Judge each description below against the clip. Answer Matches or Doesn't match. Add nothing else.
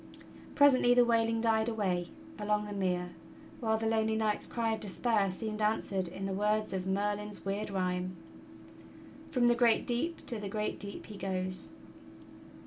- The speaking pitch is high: Matches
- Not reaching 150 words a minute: Doesn't match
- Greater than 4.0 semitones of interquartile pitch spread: Doesn't match